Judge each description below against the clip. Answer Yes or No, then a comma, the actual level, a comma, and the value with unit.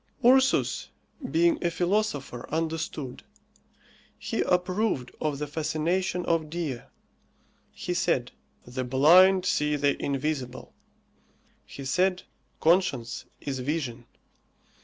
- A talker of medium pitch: Yes, medium, 155 Hz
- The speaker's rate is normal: No, slow, 95 wpm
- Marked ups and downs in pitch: No, average, 4.8 semitones